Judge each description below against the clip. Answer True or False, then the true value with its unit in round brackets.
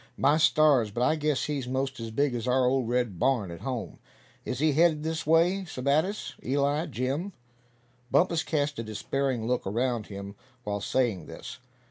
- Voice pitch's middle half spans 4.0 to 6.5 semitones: True (4.5 semitones)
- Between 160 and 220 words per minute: True (170 wpm)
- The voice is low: True (130 Hz)